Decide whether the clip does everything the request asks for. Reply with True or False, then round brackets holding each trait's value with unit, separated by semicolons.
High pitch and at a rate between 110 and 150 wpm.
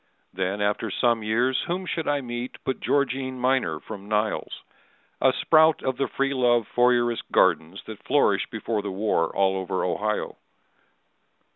False (120 Hz; 145 wpm)